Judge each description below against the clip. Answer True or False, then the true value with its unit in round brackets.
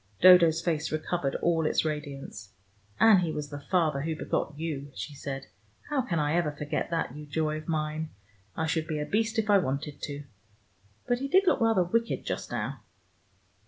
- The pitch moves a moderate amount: True (3.3 semitones)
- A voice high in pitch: False (155 Hz)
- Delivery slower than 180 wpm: False (190 wpm)